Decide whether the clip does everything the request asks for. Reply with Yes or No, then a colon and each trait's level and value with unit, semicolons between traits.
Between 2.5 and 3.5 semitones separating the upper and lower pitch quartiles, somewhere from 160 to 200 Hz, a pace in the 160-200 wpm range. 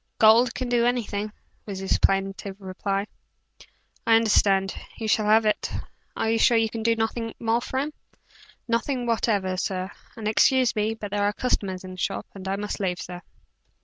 No: average, 2.8 semitones; high, 215 Hz; average, 180 wpm